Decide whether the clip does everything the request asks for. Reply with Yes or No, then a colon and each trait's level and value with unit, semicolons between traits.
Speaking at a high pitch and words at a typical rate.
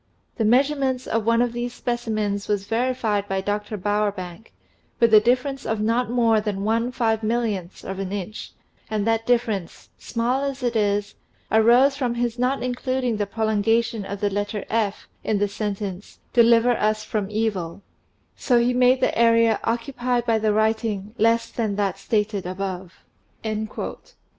Yes: high, 220 Hz; average, 155 wpm